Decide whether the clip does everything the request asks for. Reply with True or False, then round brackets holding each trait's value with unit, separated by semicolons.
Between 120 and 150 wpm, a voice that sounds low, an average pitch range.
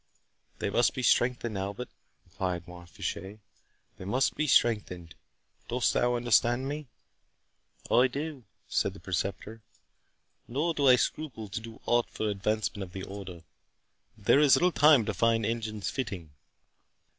True (145 wpm; 115 Hz; 4.4 semitones)